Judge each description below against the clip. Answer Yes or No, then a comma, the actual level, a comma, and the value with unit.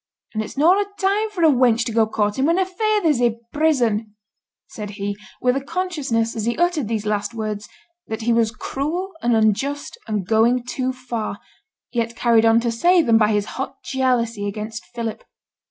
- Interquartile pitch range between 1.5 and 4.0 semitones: No, average, 4.6 semitones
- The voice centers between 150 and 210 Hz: No, high, 235 Hz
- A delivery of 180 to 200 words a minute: Yes, average, 185 wpm